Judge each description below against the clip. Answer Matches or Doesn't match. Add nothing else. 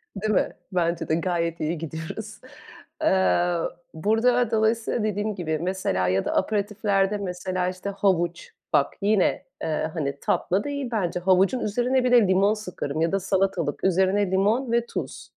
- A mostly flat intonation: Doesn't match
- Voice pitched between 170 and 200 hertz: Matches